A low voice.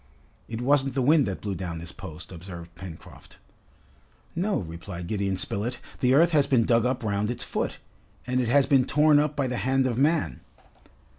Yes: low, 120 Hz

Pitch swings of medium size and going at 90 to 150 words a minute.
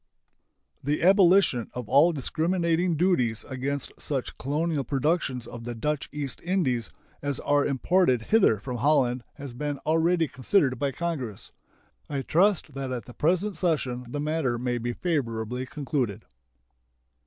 Yes: average, 4.9 semitones; average, 140 wpm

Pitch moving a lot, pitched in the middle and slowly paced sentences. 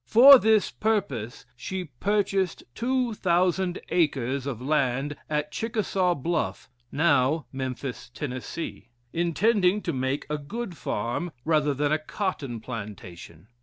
Yes: wide, 6.3 semitones; medium, 155 Hz; slow, 120 wpm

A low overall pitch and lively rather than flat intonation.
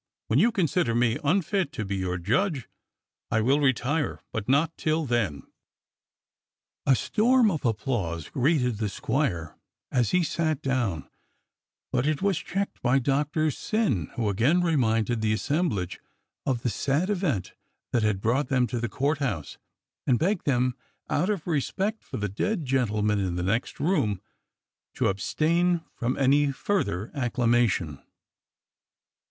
Yes: low, 130 Hz; wide, 6.5 semitones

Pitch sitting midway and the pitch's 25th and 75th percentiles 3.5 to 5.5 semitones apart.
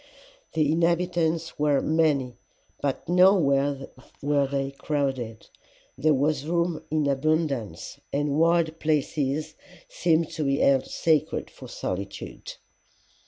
No: medium, 150 Hz; average, 2.8 semitones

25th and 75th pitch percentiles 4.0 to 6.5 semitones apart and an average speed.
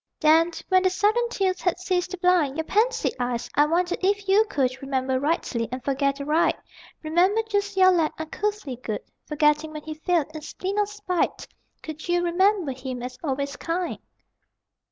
Yes: average, 5.0 semitones; average, 175 wpm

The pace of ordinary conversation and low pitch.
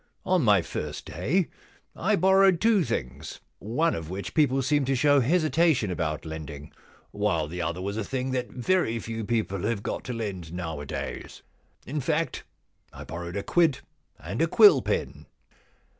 Yes: average, 165 wpm; low, 115 Hz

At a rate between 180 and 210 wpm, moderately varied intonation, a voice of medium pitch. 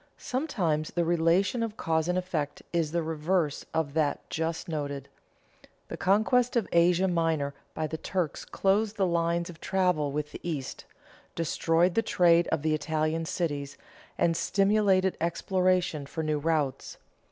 No: average, 155 wpm; average, 3.1 semitones; medium, 165 Hz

